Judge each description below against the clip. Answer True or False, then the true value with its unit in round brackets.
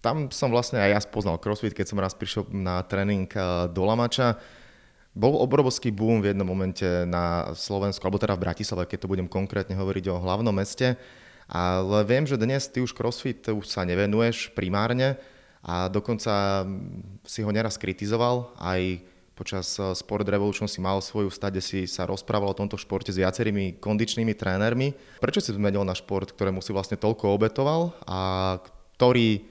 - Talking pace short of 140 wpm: False (165 wpm)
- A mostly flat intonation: False (3.4 semitones)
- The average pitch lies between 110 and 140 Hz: False (100 Hz)